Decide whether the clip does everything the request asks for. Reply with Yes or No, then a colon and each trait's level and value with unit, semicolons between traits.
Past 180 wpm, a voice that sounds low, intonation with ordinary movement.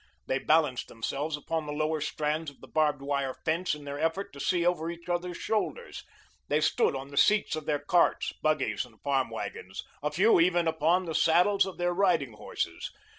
No: average, 195 wpm; medium, 155 Hz; average, 3.4 semitones